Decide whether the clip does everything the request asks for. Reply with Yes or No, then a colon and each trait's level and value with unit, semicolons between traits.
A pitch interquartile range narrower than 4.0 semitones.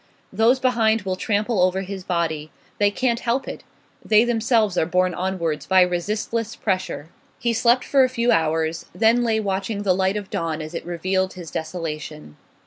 No: average, 4.8 semitones